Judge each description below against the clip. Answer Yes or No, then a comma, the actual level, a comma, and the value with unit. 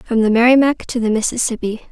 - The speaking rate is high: No, average, 190 wpm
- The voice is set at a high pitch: Yes, high, 235 Hz